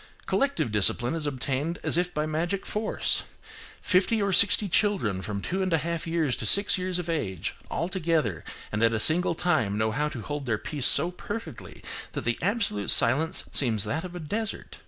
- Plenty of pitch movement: Yes, wide, 7.4 semitones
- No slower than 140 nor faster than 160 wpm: No, average, 195 wpm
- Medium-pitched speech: Yes, medium, 160 Hz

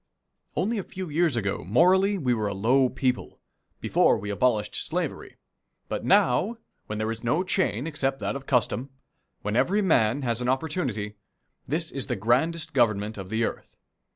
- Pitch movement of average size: No, wide, 6.7 semitones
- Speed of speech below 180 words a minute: Yes, average, 170 wpm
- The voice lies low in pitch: Yes, low, 125 Hz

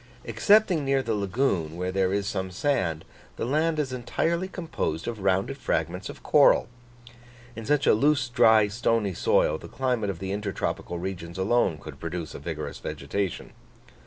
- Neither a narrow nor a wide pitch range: No, wide, 6.2 semitones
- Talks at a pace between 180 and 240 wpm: No, average, 160 wpm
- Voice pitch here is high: No, low, 105 Hz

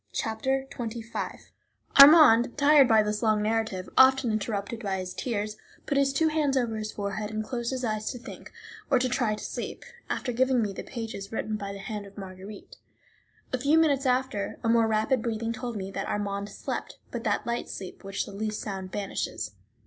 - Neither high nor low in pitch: No, high, 220 Hz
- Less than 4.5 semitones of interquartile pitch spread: Yes, average, 3.7 semitones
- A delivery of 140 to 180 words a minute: No, average, 195 wpm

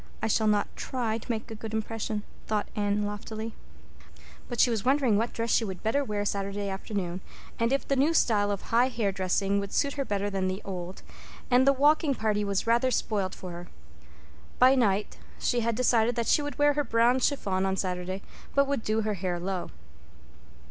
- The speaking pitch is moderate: No, high, 220 Hz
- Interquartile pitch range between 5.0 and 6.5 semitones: No, average, 3.6 semitones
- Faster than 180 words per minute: Yes, average, 200 wpm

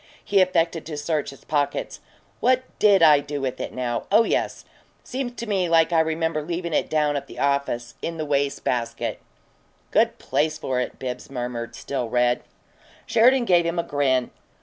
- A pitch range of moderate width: Yes, average, 4.4 semitones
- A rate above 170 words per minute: Yes, average, 180 wpm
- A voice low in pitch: No, medium, 150 Hz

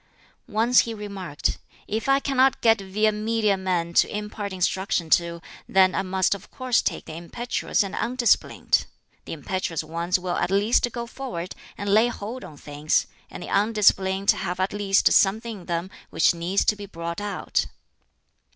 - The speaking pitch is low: No, high, 195 Hz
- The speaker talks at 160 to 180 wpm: Yes, average, 170 wpm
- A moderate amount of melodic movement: Yes, average, 3.6 semitones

